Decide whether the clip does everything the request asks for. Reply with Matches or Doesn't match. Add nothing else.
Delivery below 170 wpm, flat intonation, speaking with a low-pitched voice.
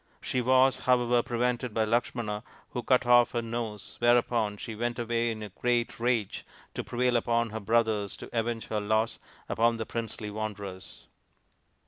Matches